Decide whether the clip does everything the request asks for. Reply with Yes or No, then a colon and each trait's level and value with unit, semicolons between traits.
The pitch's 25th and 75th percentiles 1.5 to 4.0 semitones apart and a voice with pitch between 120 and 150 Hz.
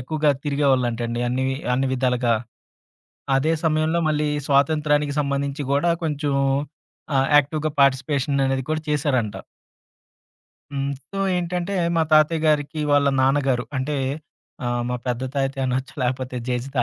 Yes: narrow, 2.6 semitones; medium, 140 Hz